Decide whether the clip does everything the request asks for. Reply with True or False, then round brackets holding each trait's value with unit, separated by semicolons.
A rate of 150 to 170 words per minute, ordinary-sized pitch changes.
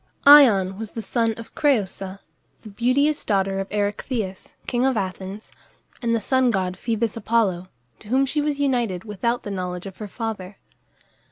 True (165 wpm; 4.1 semitones)